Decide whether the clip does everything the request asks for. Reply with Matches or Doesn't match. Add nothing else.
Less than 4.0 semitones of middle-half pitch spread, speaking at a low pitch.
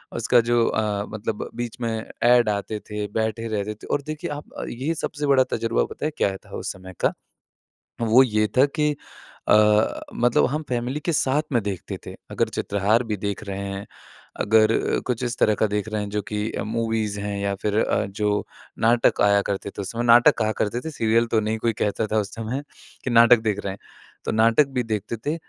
Matches